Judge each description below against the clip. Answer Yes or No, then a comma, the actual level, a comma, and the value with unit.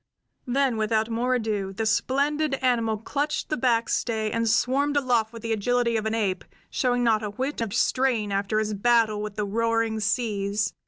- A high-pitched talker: Yes, high, 230 Hz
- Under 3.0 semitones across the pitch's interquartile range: Yes, narrow, 2.6 semitones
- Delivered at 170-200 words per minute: Yes, average, 180 wpm